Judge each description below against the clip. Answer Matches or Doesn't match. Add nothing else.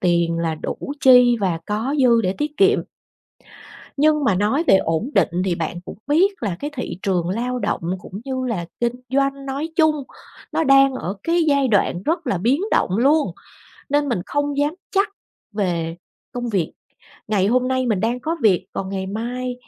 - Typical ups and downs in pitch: Doesn't match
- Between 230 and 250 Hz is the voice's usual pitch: Matches